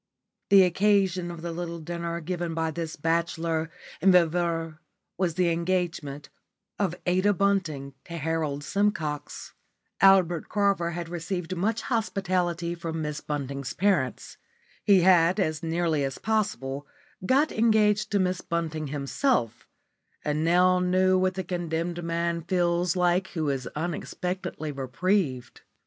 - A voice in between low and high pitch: Yes, medium, 170 Hz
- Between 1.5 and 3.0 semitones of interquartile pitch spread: Yes, average, 2.7 semitones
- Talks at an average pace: No, slow, 130 wpm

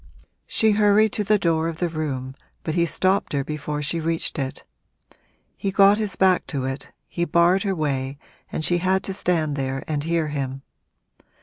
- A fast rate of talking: No, average, 185 wpm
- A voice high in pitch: No, medium, 165 Hz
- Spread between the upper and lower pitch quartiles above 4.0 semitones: Yes, average, 4.6 semitones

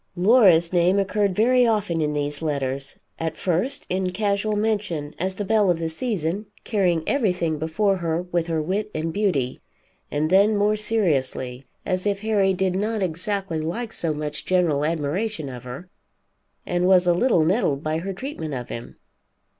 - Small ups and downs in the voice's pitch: No, average, 4.6 semitones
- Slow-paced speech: No, average, 170 wpm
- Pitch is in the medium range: Yes, medium, 180 Hz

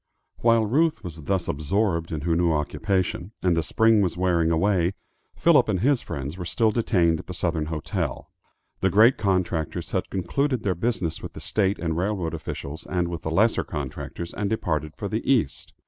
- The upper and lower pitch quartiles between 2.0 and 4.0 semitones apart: No, average, 4.7 semitones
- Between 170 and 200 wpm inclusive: Yes, average, 185 wpm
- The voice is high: No, very low, 90 Hz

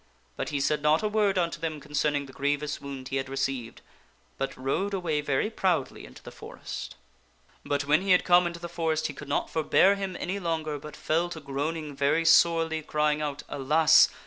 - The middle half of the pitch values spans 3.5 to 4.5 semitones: No, average, 3.0 semitones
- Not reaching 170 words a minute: No, average, 200 wpm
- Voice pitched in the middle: Yes, medium, 155 Hz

